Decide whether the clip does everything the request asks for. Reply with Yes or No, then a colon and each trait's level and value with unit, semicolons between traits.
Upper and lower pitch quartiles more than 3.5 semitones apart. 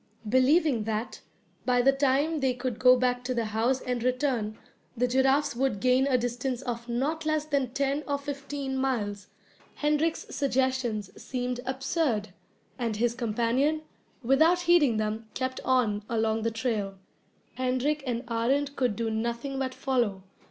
No: average, 2.9 semitones